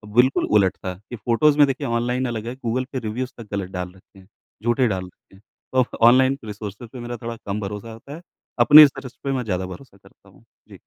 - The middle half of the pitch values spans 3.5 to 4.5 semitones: Yes, average, 4.1 semitones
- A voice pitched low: Yes, low, 120 Hz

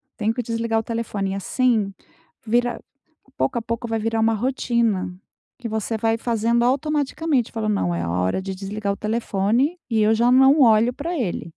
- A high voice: Yes, high, 225 Hz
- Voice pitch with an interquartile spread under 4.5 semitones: Yes, narrow, 2.4 semitones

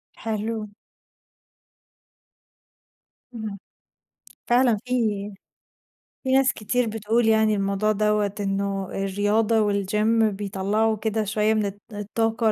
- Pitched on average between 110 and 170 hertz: No, high, 215 Hz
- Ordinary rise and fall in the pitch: No, narrow, 1.7 semitones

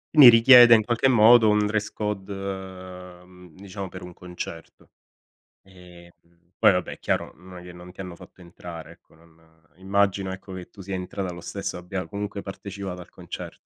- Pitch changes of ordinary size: No, narrow, 2.2 semitones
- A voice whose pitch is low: Yes, very low, 95 Hz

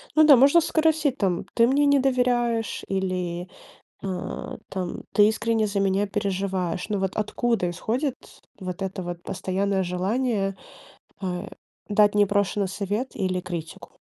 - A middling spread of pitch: Yes, average, 4.1 semitones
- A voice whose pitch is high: Yes, high, 200 Hz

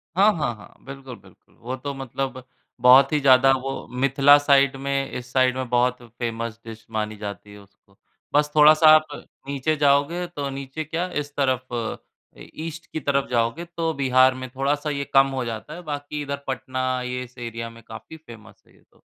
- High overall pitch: No, low, 135 Hz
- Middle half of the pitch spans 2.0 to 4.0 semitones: Yes, average, 2.9 semitones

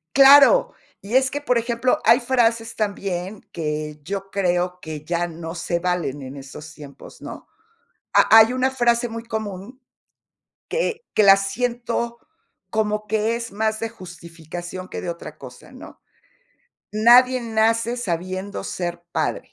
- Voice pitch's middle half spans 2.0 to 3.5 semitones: No, average, 5.2 semitones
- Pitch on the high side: Yes, high, 210 Hz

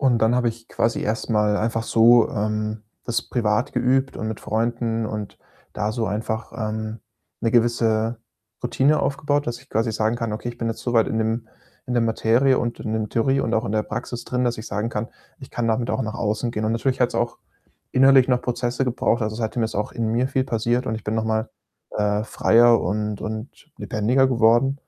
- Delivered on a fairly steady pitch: Yes, narrow, 1.9 semitones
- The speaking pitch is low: Yes, low, 115 Hz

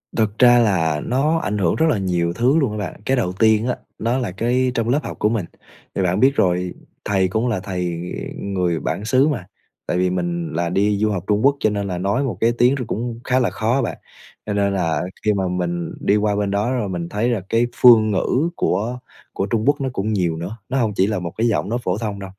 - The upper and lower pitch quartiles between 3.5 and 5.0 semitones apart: Yes, average, 4.6 semitones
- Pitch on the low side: Yes, low, 105 Hz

